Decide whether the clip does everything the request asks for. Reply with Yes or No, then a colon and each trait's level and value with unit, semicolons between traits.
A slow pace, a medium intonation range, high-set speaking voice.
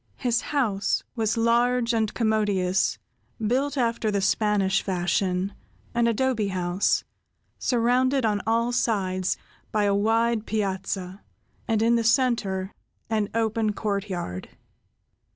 Yes: slow, 105 wpm; average, 3.1 semitones; high, 215 Hz